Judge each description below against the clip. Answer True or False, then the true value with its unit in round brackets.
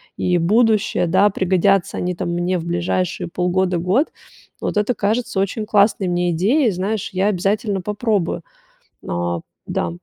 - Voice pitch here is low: False (190 Hz)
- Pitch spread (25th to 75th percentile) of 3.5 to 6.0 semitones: False (3.0 semitones)